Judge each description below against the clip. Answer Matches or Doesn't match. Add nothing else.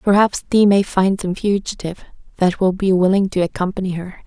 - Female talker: Matches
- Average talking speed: Matches